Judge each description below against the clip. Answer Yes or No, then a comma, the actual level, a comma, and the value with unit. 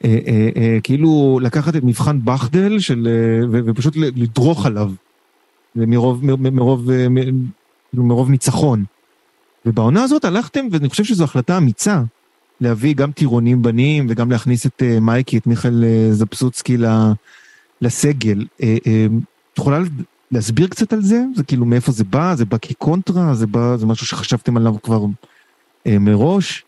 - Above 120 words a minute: No, average, 115 wpm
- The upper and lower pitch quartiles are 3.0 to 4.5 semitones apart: Yes, average, 4.2 semitones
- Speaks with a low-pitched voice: Yes, low, 125 Hz